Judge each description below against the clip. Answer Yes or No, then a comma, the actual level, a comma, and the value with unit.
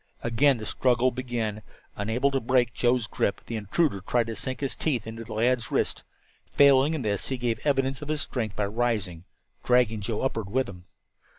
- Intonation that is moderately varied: Yes, average, 3.3 semitones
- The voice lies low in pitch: Yes, low, 120 Hz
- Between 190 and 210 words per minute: Yes, average, 195 wpm